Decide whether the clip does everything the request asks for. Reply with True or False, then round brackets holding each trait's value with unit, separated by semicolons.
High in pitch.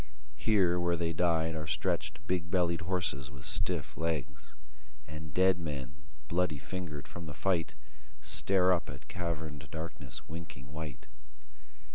False (80 Hz)